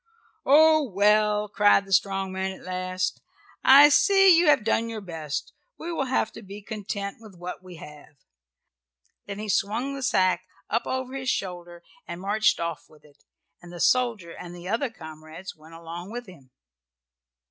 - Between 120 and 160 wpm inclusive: No, average, 170 wpm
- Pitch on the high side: Yes, high, 200 Hz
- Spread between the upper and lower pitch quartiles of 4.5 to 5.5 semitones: Yes, average, 5.1 semitones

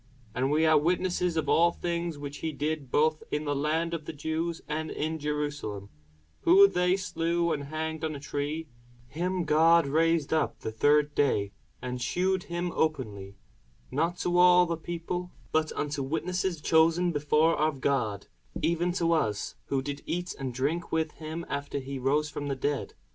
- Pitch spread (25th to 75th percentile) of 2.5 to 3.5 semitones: Yes, average, 2.9 semitones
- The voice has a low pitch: No, medium, 155 Hz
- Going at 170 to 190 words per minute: Yes, average, 175 wpm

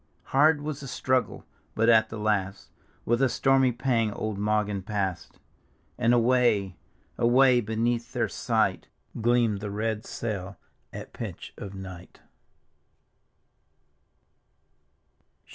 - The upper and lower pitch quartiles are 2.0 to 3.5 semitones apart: Yes, average, 3.2 semitones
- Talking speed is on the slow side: Yes, slow, 110 wpm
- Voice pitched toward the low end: Yes, low, 115 Hz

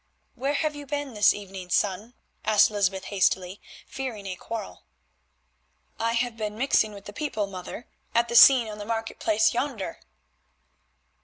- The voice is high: Yes, high, 220 Hz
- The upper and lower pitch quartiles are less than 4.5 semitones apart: Yes, average, 3.5 semitones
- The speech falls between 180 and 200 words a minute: No, average, 155 wpm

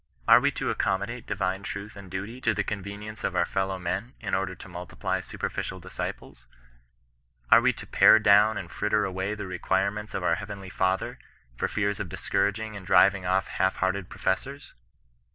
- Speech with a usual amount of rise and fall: No, narrow, 1.9 semitones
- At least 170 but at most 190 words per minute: Yes, average, 185 wpm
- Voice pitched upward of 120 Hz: No, very low, 95 Hz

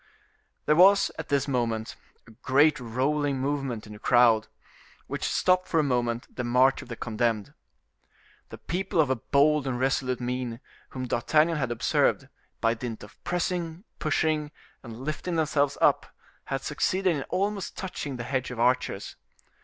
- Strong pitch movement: No, average, 4.2 semitones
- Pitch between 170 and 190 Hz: No, low, 135 Hz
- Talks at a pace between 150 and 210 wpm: Yes, average, 160 wpm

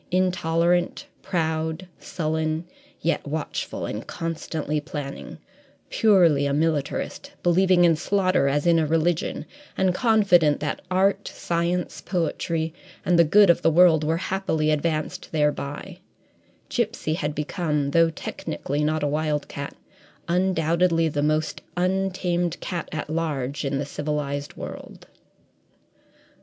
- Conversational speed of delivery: No, slow, 120 wpm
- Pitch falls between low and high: Yes, medium, 165 Hz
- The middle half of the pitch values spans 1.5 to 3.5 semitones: Yes, average, 2.9 semitones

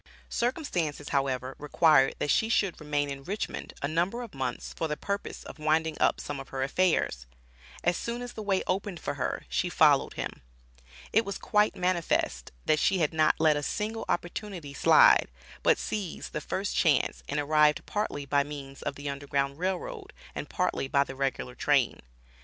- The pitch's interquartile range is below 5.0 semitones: No, average, 5.3 semitones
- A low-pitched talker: No, medium, 155 Hz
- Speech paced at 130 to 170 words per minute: No, average, 180 wpm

